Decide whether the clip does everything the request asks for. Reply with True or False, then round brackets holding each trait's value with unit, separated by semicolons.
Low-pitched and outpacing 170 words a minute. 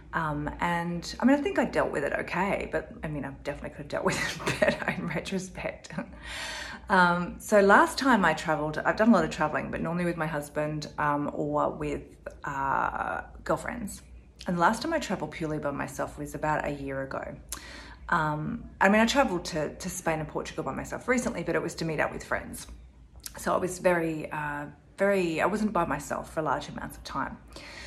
False (165 Hz; 205 wpm)